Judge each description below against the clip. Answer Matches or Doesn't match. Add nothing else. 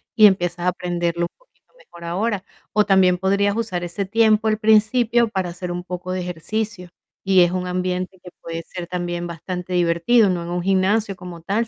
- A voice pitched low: Doesn't match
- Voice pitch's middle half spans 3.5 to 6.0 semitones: Doesn't match